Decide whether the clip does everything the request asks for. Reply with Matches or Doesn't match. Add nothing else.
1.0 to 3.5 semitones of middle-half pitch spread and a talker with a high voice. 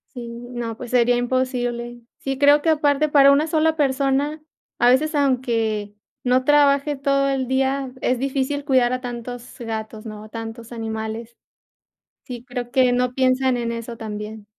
Matches